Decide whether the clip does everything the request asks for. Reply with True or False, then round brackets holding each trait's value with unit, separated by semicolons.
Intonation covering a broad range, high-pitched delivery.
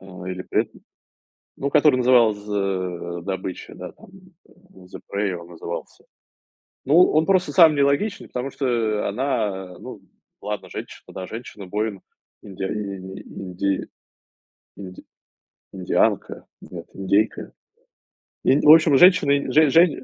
False (6.8 semitones; 105 Hz)